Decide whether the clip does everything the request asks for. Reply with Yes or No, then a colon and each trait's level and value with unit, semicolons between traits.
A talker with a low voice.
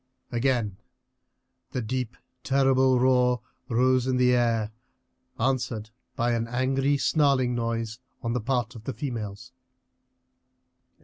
Yes: low, 125 Hz